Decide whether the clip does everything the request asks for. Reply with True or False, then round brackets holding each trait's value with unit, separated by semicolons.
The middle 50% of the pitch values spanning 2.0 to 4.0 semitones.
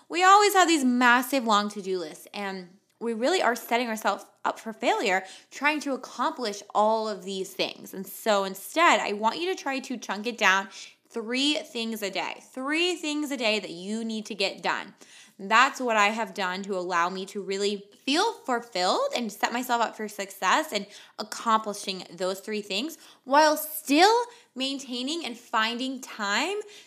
False (5.5 semitones)